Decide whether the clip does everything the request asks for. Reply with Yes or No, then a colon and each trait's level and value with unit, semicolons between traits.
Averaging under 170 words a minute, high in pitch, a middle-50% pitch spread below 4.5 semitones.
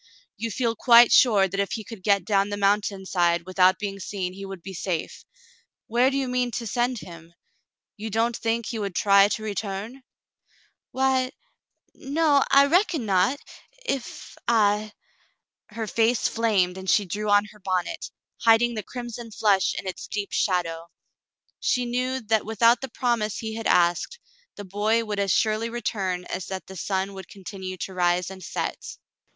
No: average, 185 wpm; high, 210 Hz; average, 3.6 semitones